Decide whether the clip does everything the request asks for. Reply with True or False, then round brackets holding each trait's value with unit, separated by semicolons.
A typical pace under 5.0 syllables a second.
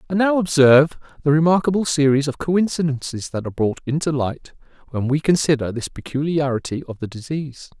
False (5.9 syllables/s)